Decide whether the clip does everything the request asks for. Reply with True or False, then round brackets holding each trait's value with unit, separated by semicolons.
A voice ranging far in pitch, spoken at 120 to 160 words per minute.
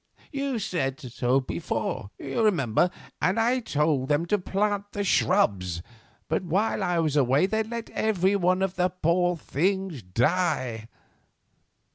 True (6.7 semitones; 140 wpm)